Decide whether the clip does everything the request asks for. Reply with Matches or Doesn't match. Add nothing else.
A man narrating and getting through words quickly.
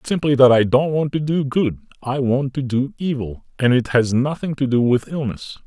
Matches